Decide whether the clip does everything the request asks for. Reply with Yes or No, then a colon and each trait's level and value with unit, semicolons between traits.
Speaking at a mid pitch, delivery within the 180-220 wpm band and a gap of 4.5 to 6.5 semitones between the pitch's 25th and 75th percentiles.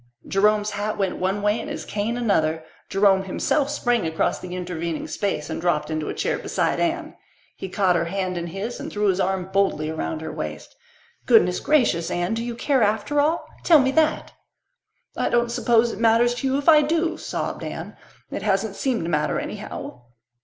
No: high, 205 Hz; average, 195 wpm; average, 5.3 semitones